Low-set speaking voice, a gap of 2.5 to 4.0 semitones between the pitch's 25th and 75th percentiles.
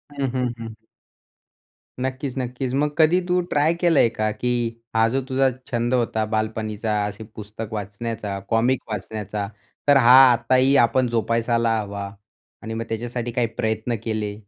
Yes: low, 115 Hz; average, 2.8 semitones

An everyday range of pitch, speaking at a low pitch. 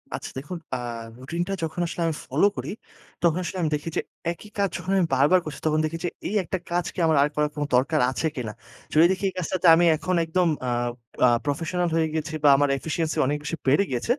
No: average, 3.2 semitones; medium, 160 Hz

